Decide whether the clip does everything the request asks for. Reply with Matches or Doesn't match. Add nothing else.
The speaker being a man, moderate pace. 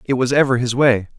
Doesn't match